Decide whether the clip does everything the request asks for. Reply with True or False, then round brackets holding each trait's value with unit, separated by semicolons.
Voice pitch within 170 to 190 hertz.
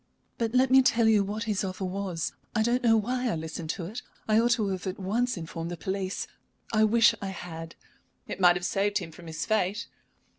False (200 Hz)